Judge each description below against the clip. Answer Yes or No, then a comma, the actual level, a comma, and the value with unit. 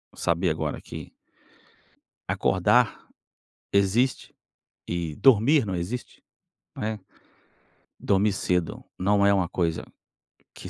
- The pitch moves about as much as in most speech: Yes, average, 3.6 semitones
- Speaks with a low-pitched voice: Yes, very low, 95 Hz